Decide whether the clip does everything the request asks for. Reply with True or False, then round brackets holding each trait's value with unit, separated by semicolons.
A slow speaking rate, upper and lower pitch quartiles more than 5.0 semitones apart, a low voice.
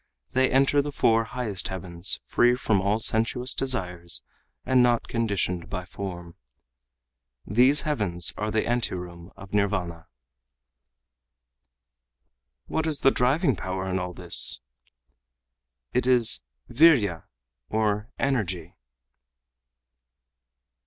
True (105 wpm; 5.6 semitones; 105 Hz)